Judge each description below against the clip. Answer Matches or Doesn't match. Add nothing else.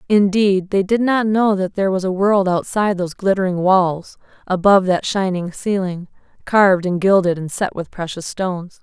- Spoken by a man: Doesn't match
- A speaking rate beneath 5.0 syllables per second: Doesn't match